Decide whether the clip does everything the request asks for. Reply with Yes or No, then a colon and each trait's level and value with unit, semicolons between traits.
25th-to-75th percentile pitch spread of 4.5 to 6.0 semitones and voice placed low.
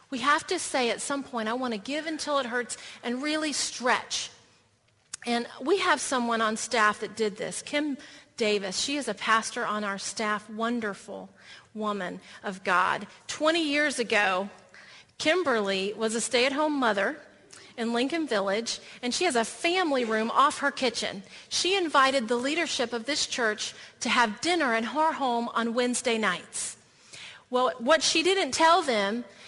No: average, 5.0 semitones; high, 240 Hz